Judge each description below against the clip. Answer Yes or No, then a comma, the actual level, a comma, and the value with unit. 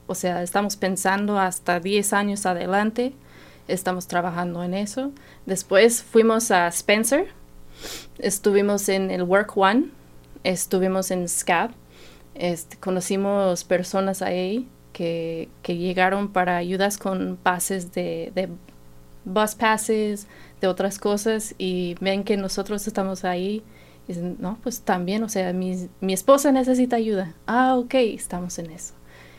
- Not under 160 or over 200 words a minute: No, slow, 135 wpm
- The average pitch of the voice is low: No, high, 190 Hz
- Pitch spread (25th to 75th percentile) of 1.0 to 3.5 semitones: Yes, narrow, 2.6 semitones